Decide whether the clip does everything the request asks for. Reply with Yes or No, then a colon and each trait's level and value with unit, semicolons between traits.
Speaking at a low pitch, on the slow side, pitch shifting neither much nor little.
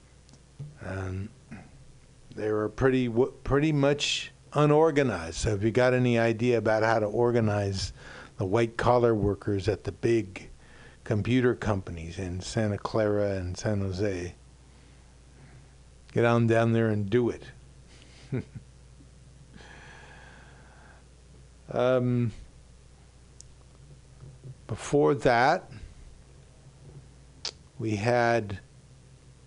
No: low, 110 Hz; slow, 95 wpm; wide, 5.7 semitones